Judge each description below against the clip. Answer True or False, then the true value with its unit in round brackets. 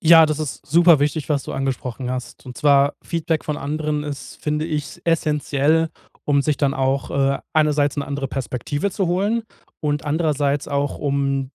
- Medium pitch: True (145 Hz)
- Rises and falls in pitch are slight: True (2.1 semitones)